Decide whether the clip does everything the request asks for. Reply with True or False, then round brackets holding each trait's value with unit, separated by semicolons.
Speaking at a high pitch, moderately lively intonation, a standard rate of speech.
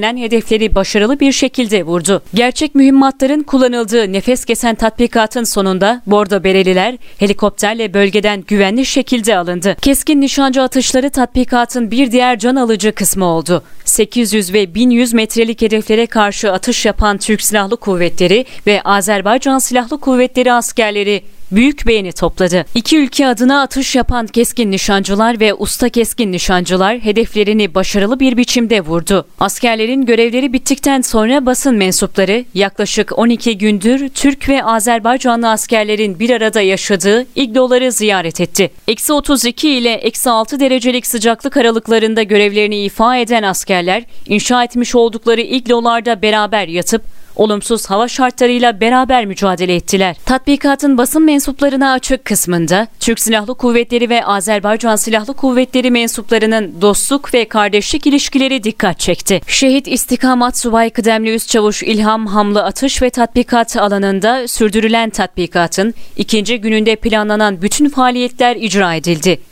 True (230 Hz; 3.3 semitones; 125 wpm)